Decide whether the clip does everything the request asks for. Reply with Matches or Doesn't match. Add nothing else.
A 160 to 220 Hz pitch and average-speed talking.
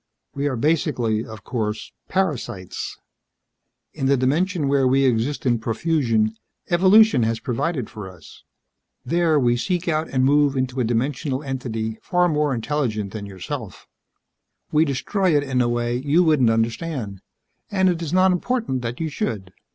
Doesn't match